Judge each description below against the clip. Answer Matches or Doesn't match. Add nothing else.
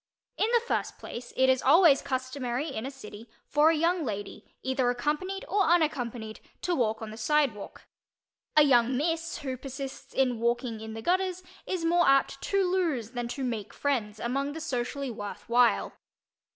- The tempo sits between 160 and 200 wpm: Matches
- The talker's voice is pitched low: Doesn't match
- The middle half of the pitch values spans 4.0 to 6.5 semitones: Matches